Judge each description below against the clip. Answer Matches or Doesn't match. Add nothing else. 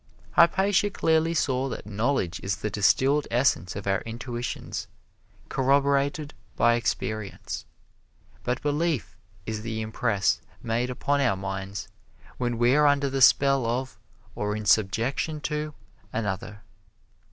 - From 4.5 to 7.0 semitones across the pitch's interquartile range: Matches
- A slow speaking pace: Matches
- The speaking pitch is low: Matches